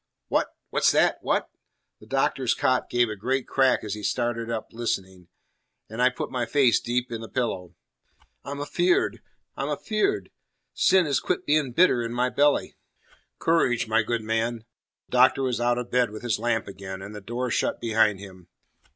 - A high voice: No, low, 120 Hz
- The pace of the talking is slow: No, average, 180 wpm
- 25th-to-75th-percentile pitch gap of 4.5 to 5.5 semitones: No, average, 2.7 semitones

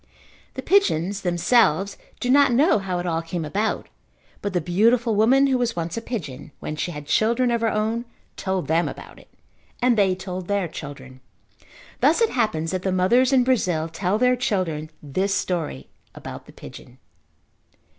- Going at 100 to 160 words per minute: No, average, 175 wpm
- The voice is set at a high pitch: Yes, high, 195 Hz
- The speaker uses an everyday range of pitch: No, wide, 5.9 semitones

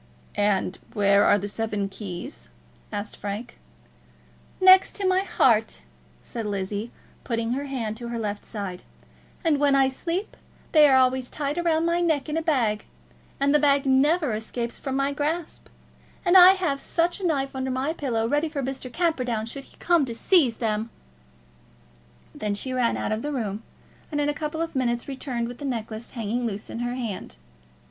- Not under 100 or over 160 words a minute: No, average, 180 wpm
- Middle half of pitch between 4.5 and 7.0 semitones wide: Yes, average, 5.0 semitones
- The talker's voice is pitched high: Yes, very high, 260 Hz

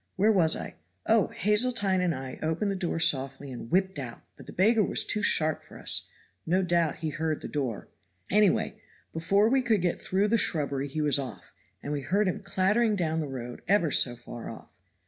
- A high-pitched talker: No, medium, 170 Hz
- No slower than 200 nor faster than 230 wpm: Yes, fast, 205 wpm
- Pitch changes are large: Yes, wide, 5.9 semitones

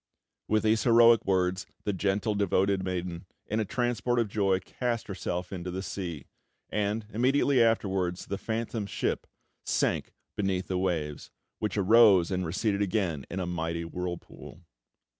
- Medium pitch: No, very low, 95 Hz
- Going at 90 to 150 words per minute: Yes, average, 145 wpm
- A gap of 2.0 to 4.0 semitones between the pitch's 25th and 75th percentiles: Yes, average, 3.4 semitones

